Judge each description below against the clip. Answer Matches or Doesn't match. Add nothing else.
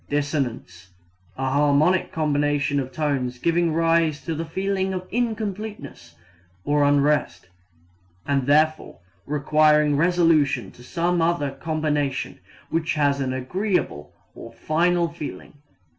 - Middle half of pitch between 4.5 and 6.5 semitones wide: Doesn't match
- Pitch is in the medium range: Matches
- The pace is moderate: Doesn't match